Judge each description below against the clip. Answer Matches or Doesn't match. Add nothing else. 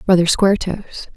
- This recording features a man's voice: Doesn't match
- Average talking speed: Matches